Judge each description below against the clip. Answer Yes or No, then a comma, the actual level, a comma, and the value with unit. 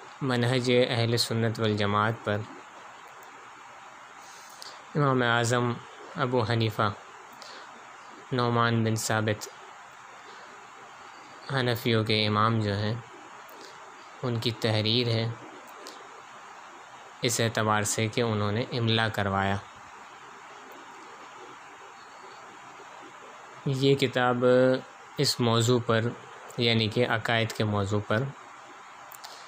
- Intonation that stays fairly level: Yes, narrow, 2.1 semitones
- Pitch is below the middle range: Yes, low, 115 Hz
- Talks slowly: Yes, slow, 80 wpm